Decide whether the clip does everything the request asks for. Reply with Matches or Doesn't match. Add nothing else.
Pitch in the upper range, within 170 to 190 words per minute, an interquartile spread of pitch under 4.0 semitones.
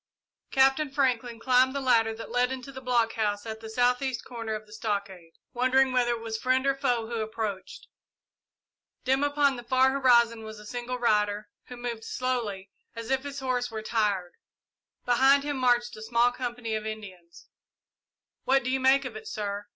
Matches